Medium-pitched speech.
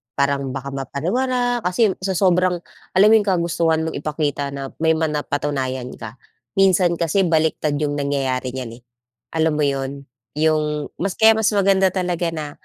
Yes: medium, 160 Hz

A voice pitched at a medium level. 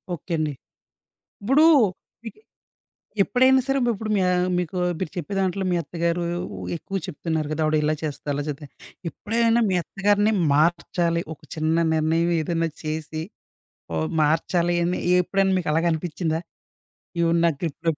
Yes: medium, 170 Hz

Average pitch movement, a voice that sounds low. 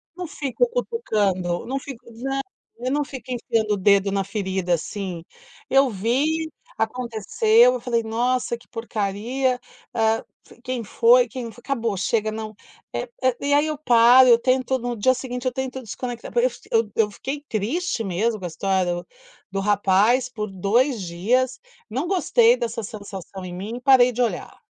No: average, 4.2 semitones; high, 235 Hz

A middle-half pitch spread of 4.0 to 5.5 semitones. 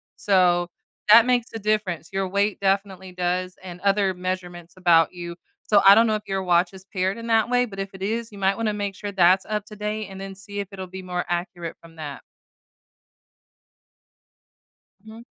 No: narrow, 2.6 semitones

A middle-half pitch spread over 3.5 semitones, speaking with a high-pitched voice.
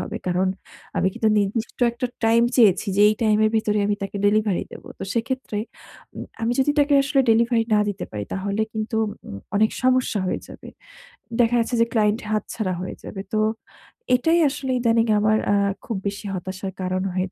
No: average, 2.8 semitones; high, 215 Hz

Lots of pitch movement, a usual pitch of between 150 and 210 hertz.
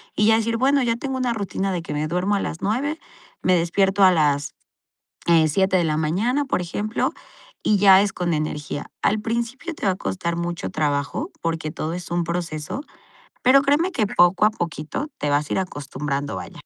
Yes: wide, 5.9 semitones; medium, 185 Hz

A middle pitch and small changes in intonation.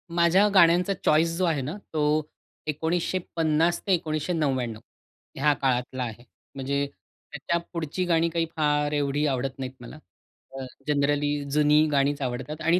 No: medium, 150 Hz; average, 3.0 semitones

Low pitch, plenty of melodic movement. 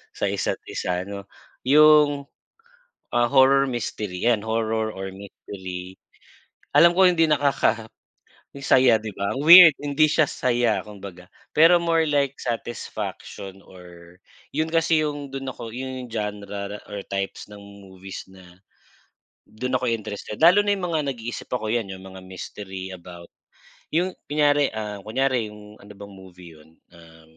Yes: low, 110 Hz; wide, 6.5 semitones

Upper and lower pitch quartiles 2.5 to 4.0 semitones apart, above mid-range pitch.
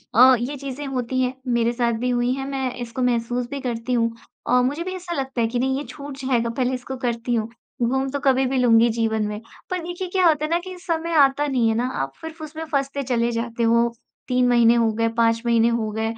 Yes: average, 2.8 semitones; very high, 250 Hz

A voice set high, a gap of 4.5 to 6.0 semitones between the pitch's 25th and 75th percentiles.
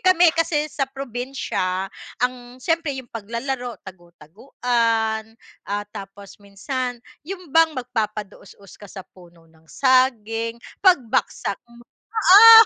Yes: high, 240 Hz; average, 5.2 semitones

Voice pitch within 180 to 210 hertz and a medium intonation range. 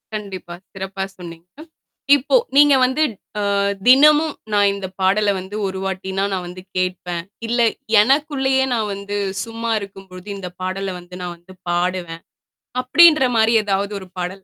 Yes: high, 195 Hz; average, 4.3 semitones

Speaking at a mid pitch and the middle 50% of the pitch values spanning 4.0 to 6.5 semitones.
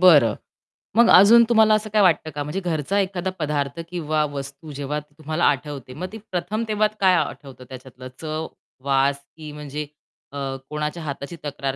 Yes: medium, 150 Hz; average, 4.5 semitones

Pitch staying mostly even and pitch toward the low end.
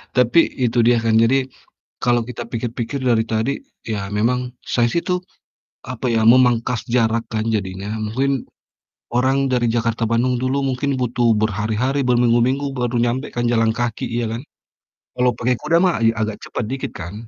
Yes: narrow, 1.9 semitones; low, 120 Hz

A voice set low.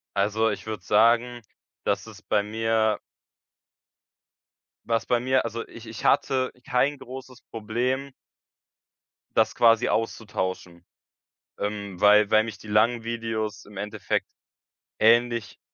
Yes: low, 110 Hz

